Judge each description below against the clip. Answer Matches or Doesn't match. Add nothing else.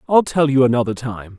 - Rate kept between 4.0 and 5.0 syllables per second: Doesn't match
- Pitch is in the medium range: Doesn't match